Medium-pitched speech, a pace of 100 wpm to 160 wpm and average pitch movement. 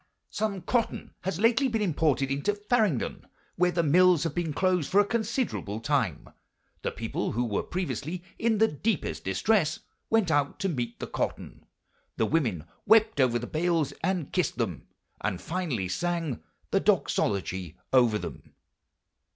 No: medium, 165 Hz; average, 150 wpm; wide, 8.1 semitones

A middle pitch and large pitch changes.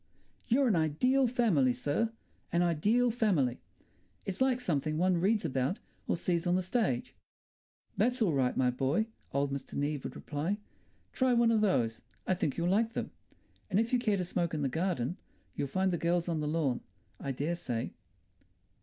Yes: medium, 175 Hz; wide, 7.4 semitones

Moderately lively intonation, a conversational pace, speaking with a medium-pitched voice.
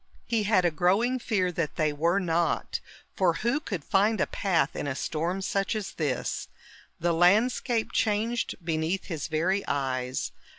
Yes: average, 4.6 semitones; average, 160 wpm; medium, 180 Hz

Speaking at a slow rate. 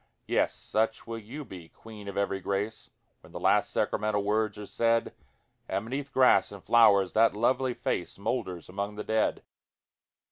No: average, 165 wpm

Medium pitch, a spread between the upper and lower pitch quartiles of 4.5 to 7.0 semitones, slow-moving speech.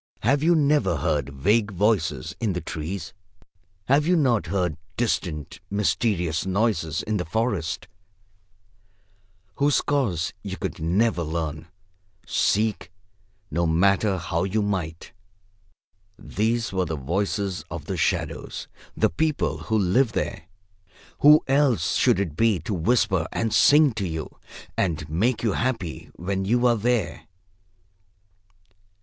No: low, 100 Hz; wide, 5.6 semitones; slow, 130 wpm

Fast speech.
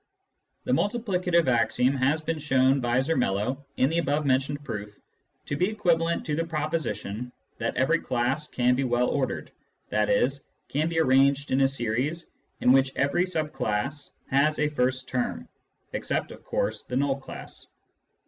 No: average, 160 wpm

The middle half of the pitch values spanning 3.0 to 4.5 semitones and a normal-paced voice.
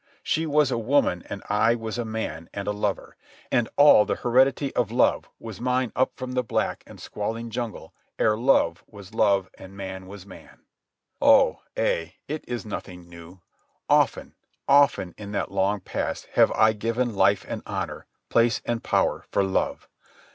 Yes: average, 3.8 semitones; average, 170 wpm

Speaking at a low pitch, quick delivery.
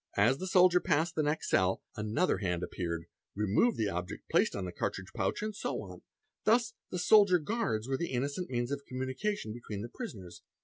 No: low, 130 Hz; average, 190 wpm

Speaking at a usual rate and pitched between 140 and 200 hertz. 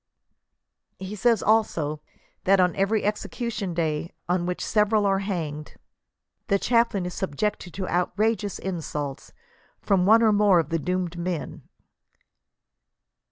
No: slow, 125 wpm; high, 190 Hz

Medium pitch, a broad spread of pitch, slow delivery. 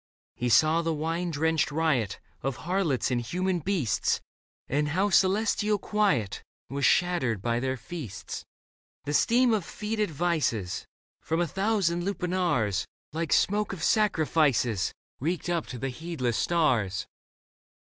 Yes: medium, 160 Hz; wide, 6.3 semitones; slow, 130 wpm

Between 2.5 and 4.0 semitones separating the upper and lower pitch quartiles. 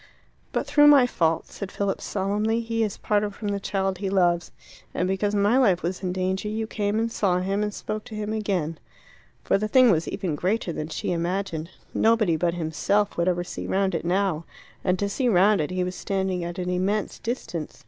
Yes: average, 2.9 semitones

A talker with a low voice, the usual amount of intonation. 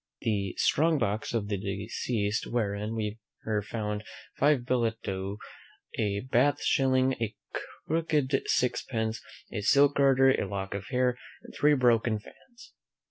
Yes: low, 115 Hz; average, 4.2 semitones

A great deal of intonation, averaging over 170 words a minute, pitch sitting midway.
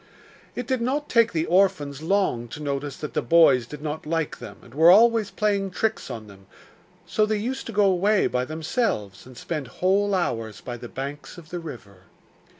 Yes: wide, 7.4 semitones; average, 195 wpm; medium, 165 Hz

